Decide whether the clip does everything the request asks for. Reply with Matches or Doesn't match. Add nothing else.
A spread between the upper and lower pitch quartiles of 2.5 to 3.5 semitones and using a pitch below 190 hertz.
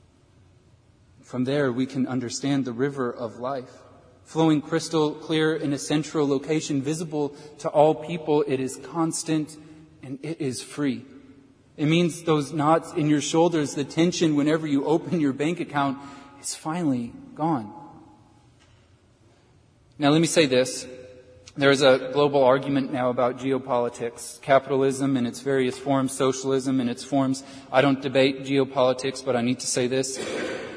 Matches